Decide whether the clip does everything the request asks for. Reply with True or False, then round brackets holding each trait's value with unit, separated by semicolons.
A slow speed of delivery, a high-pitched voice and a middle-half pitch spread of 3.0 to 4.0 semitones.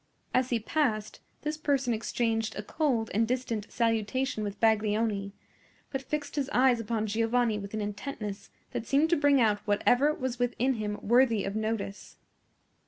False (160 wpm; 230 Hz; 3.5 semitones)